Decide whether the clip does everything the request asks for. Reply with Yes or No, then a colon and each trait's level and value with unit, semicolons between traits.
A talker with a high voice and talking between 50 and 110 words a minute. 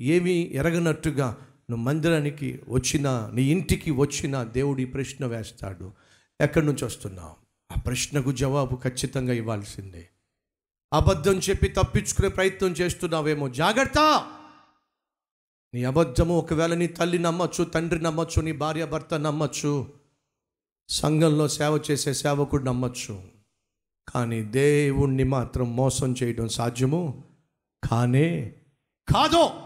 No: medium, 140 Hz; average, 100 wpm